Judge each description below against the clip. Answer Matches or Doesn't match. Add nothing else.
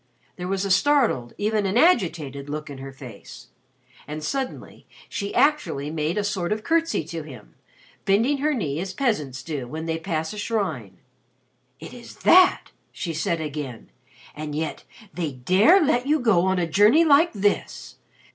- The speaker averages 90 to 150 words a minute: Doesn't match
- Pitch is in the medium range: Matches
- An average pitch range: Doesn't match